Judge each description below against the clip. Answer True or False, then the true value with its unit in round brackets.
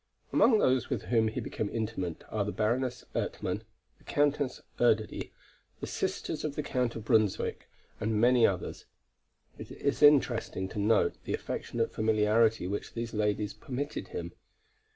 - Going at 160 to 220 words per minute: False (150 wpm)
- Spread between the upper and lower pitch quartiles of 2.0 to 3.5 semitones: True (3.0 semitones)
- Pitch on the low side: True (115 Hz)